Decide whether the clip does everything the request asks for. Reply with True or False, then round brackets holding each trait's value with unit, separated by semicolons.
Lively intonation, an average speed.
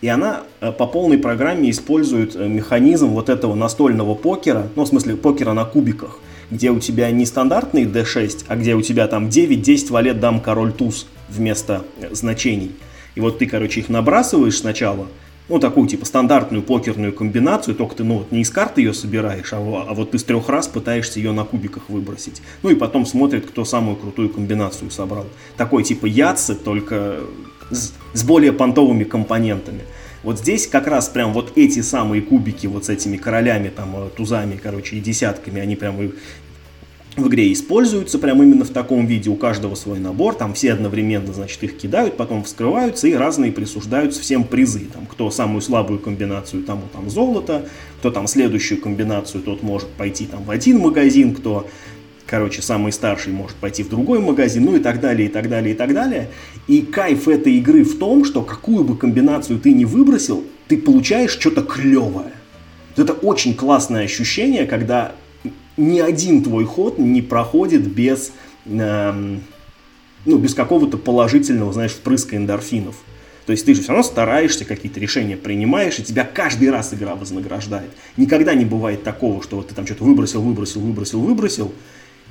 False (6.1 semitones; 175 wpm)